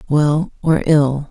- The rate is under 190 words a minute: Yes, average, 140 wpm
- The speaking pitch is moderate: Yes, medium, 150 Hz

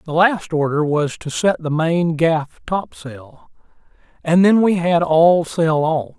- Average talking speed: Yes, average, 165 wpm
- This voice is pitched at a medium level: Yes, medium, 160 Hz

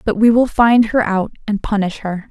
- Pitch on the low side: No, high, 215 Hz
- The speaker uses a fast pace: Yes, fast, 235 wpm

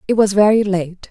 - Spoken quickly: Yes, fast, 220 wpm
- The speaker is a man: No, female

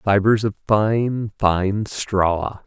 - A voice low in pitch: Yes, low, 105 Hz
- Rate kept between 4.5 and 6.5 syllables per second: No, 2.5 syllables/s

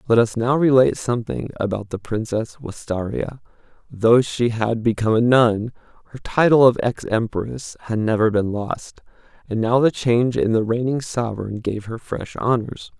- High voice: No, low, 115 Hz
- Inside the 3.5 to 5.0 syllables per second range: Yes, 4.9 syllables/s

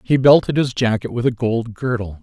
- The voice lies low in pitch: Yes, low, 120 Hz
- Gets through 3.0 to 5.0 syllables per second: No, 5.2 syllables/s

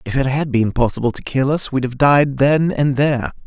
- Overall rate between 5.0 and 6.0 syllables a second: Yes, 5.2 syllables/s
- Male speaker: Yes, male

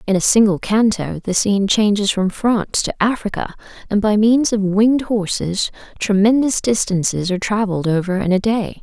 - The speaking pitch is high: Yes, high, 205 Hz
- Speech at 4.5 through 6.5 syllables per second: Yes, 5.3 syllables/s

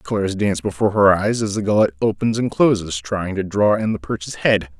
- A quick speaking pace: Yes, fast, 225 wpm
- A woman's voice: No, male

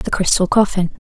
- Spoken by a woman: Yes, female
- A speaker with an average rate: Yes, average, 170 wpm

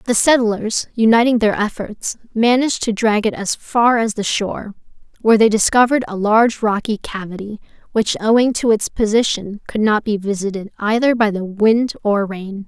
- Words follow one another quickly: No, average, 170 wpm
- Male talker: No, female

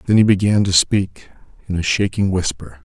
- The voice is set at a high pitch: No, very low, 95 Hz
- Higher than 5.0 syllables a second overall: Yes, 5.2 syllables/s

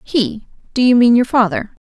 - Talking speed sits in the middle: Yes, average, 160 wpm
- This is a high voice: Yes, high, 225 Hz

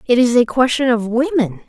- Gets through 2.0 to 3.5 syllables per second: No, 5.3 syllables/s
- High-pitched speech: Yes, high, 245 Hz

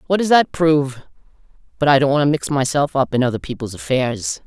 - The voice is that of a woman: Yes, female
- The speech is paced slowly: No, average, 200 wpm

